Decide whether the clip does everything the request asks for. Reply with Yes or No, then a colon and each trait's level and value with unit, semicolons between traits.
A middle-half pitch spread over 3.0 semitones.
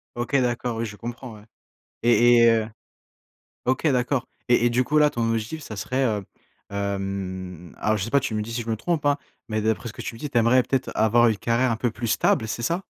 No: narrow, 2.5 semitones